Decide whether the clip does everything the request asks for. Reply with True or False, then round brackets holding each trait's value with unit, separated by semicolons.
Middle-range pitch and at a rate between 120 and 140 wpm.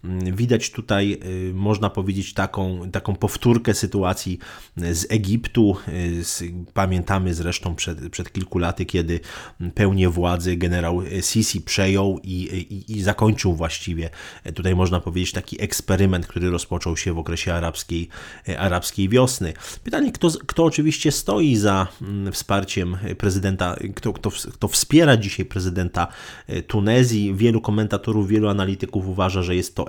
False (95 Hz; 125 wpm)